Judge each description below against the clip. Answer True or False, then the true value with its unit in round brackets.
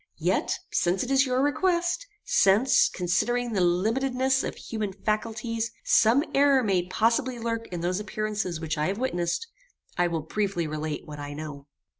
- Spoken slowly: False (160 wpm)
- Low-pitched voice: False (215 Hz)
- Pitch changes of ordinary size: False (6.3 semitones)